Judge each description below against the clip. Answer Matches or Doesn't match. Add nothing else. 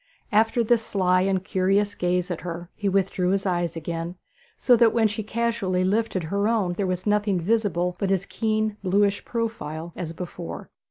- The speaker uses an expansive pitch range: Doesn't match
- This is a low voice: Doesn't match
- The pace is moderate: Matches